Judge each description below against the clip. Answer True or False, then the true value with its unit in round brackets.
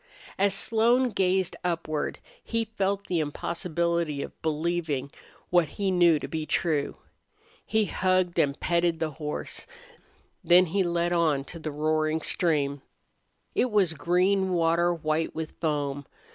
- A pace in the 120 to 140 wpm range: True (135 wpm)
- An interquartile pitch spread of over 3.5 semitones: False (3.1 semitones)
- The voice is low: False (170 Hz)